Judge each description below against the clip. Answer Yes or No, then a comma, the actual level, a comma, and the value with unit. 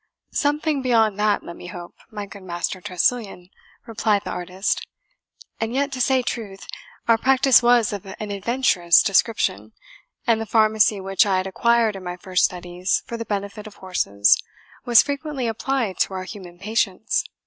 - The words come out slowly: No, average, 165 wpm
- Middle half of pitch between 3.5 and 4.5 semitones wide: Yes, average, 4.0 semitones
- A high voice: Yes, high, 210 Hz